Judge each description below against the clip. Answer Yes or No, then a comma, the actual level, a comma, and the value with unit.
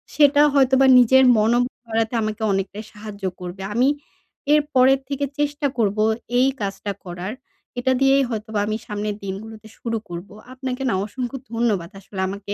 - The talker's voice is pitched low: No, high, 220 Hz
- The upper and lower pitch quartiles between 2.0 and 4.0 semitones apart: No, average, 4.5 semitones